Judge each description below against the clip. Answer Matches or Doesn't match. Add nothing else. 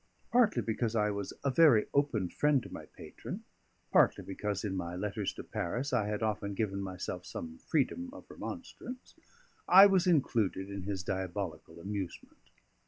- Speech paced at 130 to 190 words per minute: Matches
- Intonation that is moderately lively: Doesn't match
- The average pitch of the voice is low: Matches